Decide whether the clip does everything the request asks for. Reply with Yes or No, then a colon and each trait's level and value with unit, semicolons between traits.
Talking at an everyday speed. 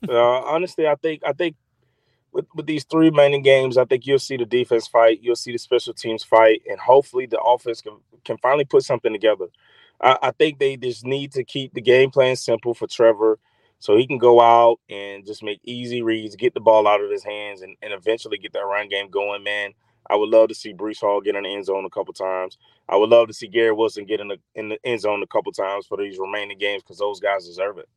No: fast, 250 wpm